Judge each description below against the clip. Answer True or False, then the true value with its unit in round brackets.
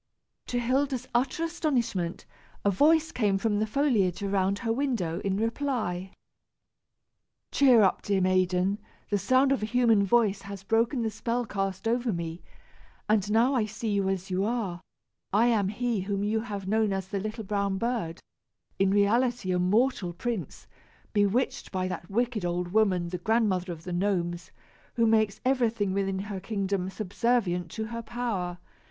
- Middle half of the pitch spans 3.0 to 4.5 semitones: True (3.8 semitones)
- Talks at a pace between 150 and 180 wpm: True (160 wpm)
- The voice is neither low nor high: False (205 Hz)